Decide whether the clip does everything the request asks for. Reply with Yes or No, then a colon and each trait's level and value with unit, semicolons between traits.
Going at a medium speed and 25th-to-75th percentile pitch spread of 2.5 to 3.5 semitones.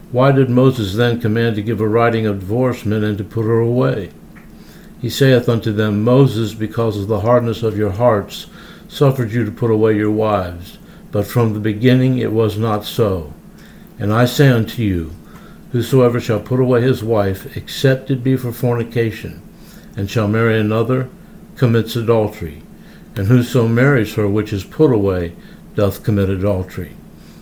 Yes: average, 165 wpm; average, 3.2 semitones